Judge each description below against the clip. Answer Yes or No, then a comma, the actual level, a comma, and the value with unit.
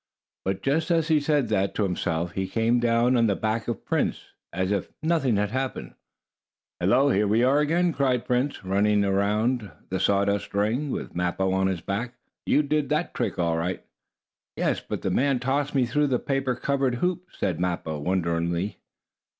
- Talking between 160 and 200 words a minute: Yes, average, 185 wpm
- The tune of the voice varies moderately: No, wide, 6.2 semitones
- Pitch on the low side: Yes, low, 115 Hz